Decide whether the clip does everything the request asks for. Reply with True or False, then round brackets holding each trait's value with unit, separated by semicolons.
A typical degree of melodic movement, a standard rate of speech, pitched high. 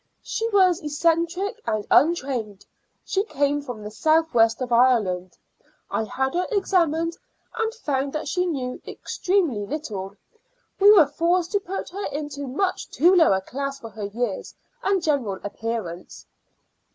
False (7.6 semitones; 150 wpm; 290 Hz)